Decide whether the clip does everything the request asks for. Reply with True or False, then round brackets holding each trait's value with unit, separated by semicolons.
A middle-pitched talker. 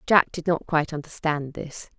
True (160 Hz)